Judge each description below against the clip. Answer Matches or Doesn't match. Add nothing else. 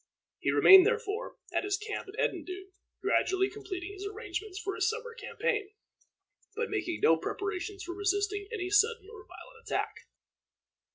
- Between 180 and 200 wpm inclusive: Doesn't match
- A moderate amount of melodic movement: Doesn't match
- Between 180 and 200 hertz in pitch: Doesn't match